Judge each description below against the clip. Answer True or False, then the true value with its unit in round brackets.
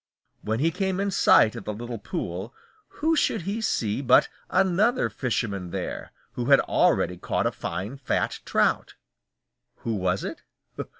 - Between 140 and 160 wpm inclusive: True (155 wpm)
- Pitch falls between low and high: False (125 Hz)